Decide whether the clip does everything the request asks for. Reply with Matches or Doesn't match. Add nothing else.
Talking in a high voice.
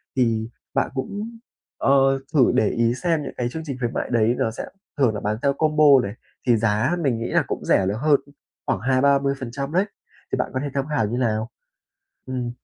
Doesn't match